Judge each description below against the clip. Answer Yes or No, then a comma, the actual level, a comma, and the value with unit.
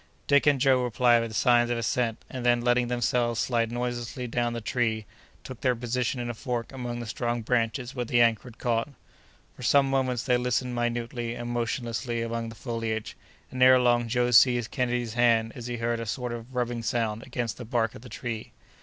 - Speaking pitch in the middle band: No, low, 120 Hz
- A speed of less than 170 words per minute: No, fast, 205 wpm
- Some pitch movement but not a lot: No, narrow, 1.2 semitones